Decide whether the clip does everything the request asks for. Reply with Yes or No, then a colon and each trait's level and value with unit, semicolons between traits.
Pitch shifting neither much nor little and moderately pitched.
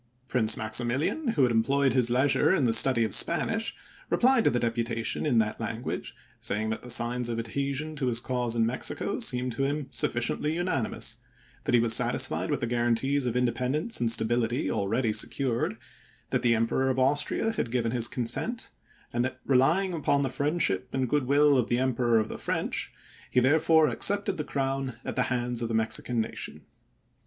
No: average, 3.3 semitones; low, 125 Hz